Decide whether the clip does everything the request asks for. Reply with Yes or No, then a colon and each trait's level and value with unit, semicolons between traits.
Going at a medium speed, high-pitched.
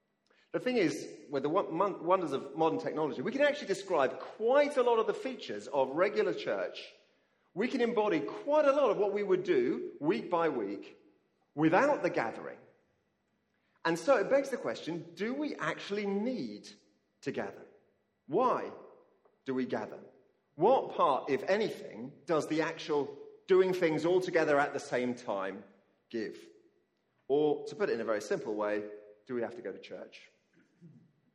Yes: average, 165 wpm; high, 215 Hz